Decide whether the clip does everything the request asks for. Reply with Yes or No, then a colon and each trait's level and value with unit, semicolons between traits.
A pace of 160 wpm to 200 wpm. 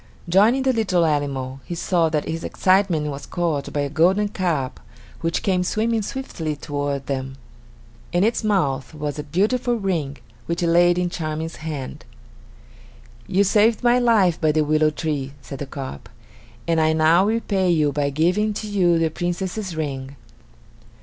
Yes: average, 165 wpm